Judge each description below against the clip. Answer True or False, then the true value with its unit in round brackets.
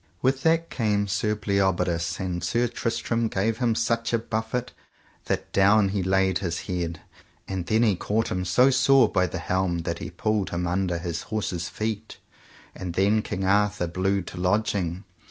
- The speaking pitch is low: True (100 Hz)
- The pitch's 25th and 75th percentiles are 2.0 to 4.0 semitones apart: True (3.5 semitones)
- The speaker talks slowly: False (170 wpm)